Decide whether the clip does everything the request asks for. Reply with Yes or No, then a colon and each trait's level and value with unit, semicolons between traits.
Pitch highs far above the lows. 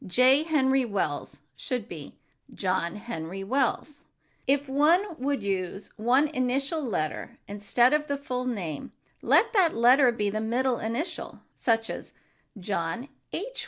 Yes: wide, 5.8 semitones